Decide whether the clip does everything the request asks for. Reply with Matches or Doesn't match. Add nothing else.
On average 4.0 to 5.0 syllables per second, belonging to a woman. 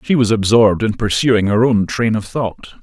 Doesn't match